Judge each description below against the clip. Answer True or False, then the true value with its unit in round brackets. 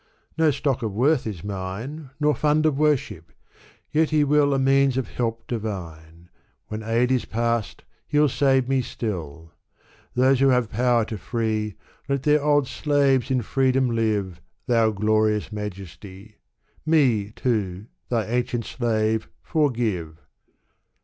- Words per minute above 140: False (135 wpm)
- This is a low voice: True (120 Hz)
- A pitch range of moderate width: True (4.4 semitones)